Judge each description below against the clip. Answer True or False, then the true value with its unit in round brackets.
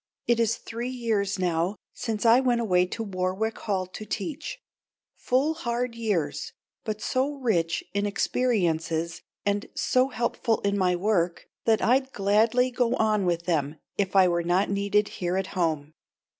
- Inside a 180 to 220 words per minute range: False (155 wpm)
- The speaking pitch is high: True (205 Hz)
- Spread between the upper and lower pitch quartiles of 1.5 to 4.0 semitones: False (4.6 semitones)